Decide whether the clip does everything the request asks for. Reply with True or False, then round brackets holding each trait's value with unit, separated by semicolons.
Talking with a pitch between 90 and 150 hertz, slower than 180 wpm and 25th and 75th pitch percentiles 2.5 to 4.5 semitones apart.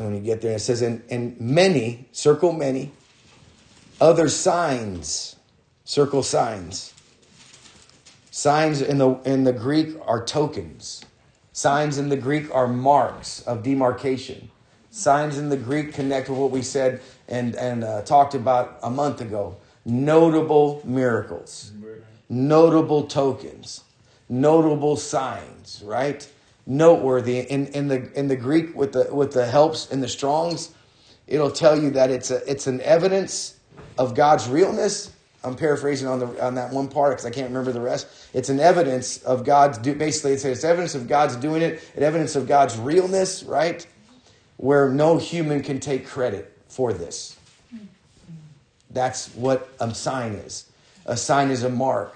True (135 Hz; 155 wpm; 2.8 semitones)